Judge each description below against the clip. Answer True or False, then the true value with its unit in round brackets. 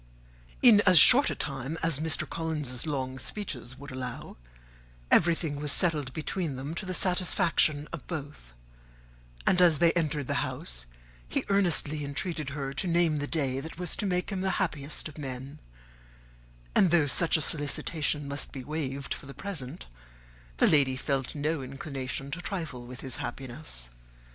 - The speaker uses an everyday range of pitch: True (3.8 semitones)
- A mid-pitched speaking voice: True (150 Hz)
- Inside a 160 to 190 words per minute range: True (165 wpm)